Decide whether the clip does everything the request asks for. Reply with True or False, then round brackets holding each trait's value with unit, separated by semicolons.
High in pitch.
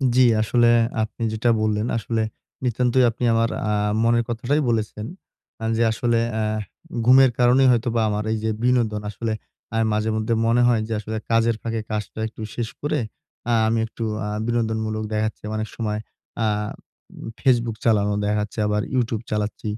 False (115 Hz)